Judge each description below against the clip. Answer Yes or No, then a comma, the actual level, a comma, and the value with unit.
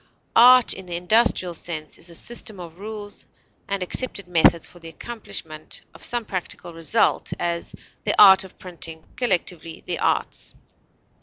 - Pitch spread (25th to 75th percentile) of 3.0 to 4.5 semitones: Yes, average, 4.0 semitones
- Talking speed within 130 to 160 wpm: Yes, average, 150 wpm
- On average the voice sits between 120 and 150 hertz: No, medium, 180 Hz